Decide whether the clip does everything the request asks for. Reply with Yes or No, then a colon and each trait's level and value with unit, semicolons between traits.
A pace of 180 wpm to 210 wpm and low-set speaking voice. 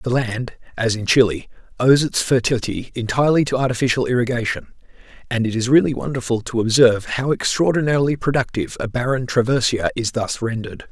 No: average, 155 wpm; low, 120 Hz